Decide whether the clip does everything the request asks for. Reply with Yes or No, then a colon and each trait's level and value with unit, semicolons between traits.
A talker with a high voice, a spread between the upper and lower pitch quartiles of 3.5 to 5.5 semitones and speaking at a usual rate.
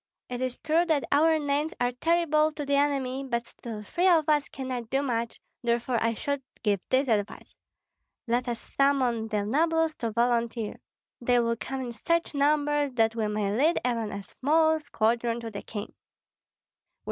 Yes: very high, 255 Hz; average, 4.1 semitones; average, 170 wpm